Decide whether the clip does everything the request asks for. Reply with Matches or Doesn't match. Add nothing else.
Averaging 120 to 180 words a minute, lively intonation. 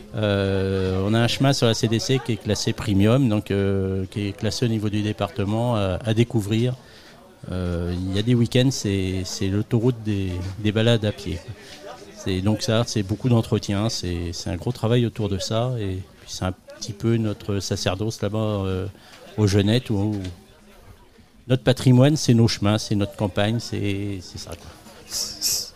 Doesn't match